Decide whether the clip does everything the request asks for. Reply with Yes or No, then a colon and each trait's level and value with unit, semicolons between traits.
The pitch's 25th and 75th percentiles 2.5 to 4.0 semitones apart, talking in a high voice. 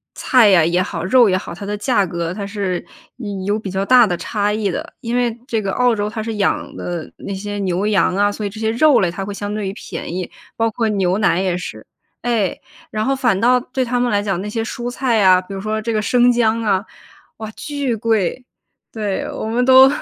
Yes: average, 3.3 semitones; high, 210 Hz